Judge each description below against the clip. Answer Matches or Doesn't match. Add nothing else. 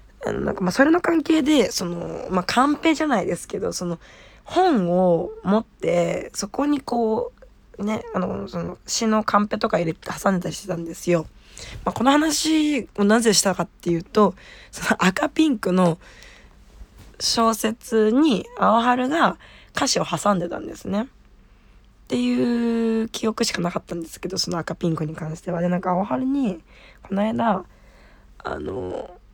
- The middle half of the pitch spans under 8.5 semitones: Matches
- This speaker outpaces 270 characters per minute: Matches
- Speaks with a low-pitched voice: Doesn't match